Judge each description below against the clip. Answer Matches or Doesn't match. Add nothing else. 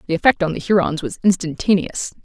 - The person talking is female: Matches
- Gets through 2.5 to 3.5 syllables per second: Doesn't match